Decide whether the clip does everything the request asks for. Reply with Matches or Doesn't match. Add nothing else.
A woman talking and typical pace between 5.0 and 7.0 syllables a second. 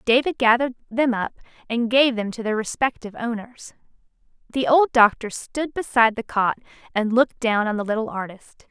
Matches